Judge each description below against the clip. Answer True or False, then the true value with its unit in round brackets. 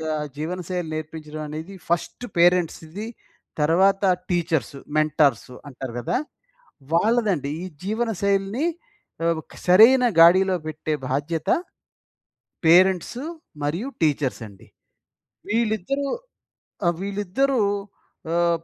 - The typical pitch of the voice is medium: True (175 Hz)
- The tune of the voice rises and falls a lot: False (4.3 semitones)